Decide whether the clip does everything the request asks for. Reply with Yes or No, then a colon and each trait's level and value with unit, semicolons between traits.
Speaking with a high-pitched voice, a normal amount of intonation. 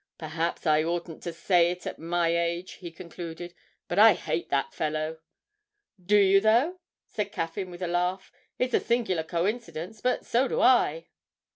No: medium, 175 Hz; average, 3.6 semitones